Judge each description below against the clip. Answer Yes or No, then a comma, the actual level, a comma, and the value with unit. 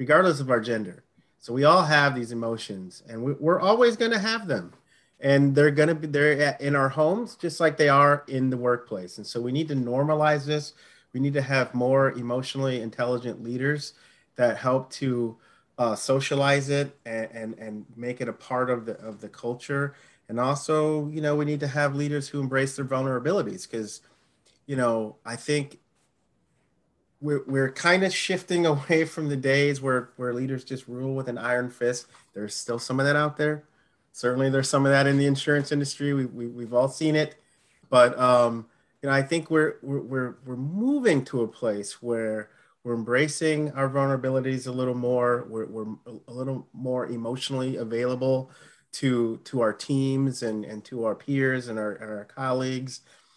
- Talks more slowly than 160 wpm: No, average, 185 wpm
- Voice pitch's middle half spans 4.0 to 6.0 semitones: No, average, 3.1 semitones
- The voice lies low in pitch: Yes, low, 130 Hz